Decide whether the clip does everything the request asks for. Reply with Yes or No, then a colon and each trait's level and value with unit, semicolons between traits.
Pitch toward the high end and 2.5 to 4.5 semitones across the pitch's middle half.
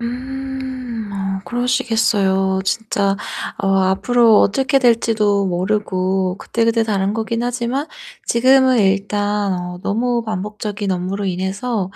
Yes: high, 210 Hz; average, 3.8 semitones